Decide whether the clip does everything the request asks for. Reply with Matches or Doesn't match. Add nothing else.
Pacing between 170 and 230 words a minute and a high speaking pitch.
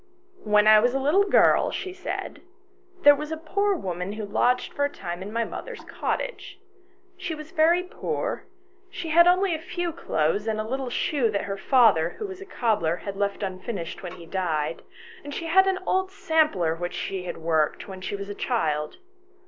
Matches